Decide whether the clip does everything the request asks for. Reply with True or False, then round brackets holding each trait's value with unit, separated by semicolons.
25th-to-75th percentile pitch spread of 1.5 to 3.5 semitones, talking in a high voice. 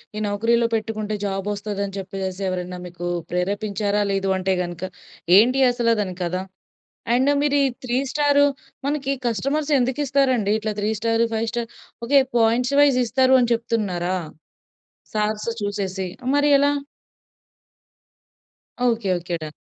False (4.5 semitones; 215 Hz)